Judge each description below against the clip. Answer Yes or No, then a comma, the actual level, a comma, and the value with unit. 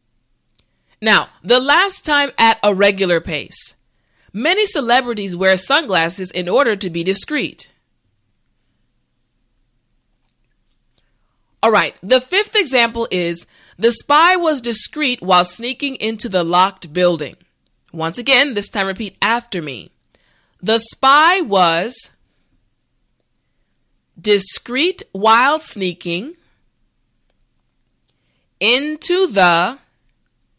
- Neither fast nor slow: No, slow, 95 wpm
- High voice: Yes, high, 220 Hz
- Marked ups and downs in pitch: Yes, wide, 7.6 semitones